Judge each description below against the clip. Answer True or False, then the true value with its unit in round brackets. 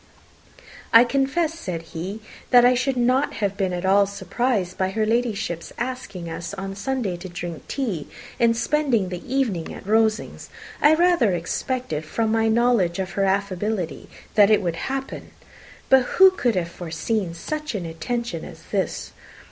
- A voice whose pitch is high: True (210 Hz)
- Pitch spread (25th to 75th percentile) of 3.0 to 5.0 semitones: False (5.4 semitones)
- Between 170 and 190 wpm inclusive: False (160 wpm)